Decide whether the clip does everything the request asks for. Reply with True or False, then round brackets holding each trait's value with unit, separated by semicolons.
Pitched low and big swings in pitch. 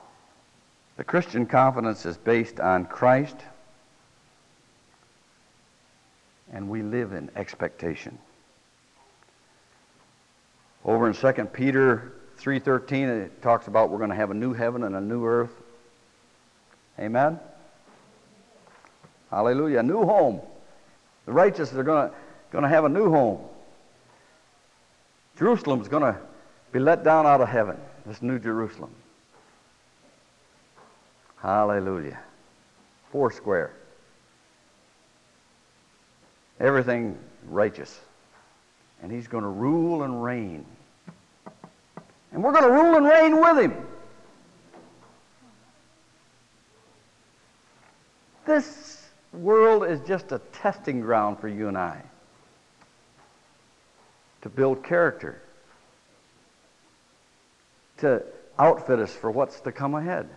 True (125 Hz; 6.0 semitones)